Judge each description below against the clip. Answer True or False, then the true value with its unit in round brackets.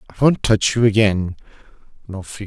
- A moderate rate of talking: True (145 wpm)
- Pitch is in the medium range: False (105 Hz)